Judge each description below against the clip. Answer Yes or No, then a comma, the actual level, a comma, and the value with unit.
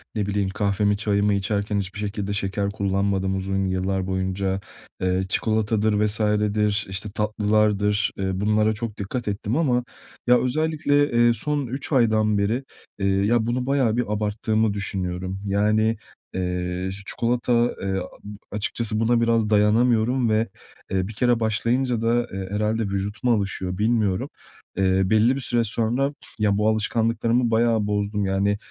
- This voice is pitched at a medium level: No, low, 105 Hz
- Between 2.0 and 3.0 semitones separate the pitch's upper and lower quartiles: Yes, average, 2.7 semitones